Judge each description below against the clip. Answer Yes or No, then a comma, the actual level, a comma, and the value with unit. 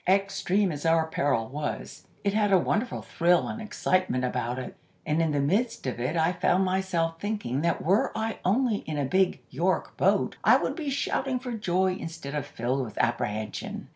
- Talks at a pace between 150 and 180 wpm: No, average, 190 wpm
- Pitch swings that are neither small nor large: No, wide, 5.8 semitones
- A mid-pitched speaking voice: Yes, medium, 175 Hz